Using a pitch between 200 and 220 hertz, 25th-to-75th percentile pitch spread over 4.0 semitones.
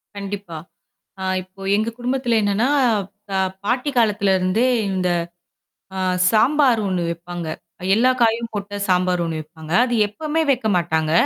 Yes: high, 205 Hz; average, 4.6 semitones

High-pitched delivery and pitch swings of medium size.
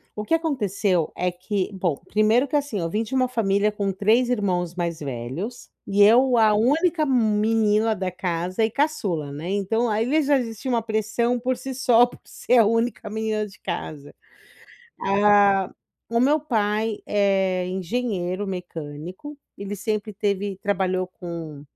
Yes: high, 210 Hz; average, 4.1 semitones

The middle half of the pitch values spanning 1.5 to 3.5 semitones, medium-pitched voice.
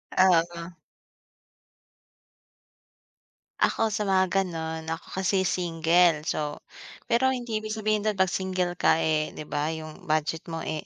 Yes: average, 3.2 semitones; medium, 175 Hz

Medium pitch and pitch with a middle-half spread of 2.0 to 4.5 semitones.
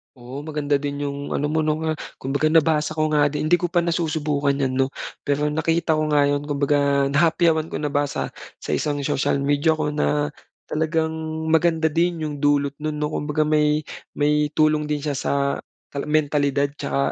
No: medium, 150 Hz; narrow, 1.5 semitones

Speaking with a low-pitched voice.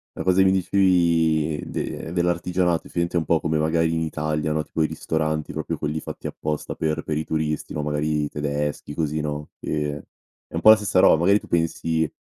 Yes: very low, 80 Hz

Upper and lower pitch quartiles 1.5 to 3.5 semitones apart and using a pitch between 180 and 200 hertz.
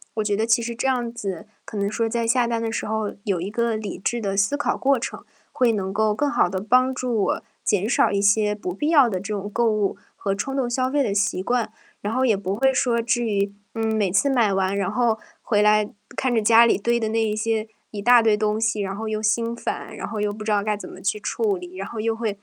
No: narrow, 2.5 semitones; high, 220 Hz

